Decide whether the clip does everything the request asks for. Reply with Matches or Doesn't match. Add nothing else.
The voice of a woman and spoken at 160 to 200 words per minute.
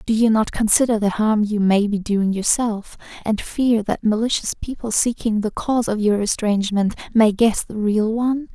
Matches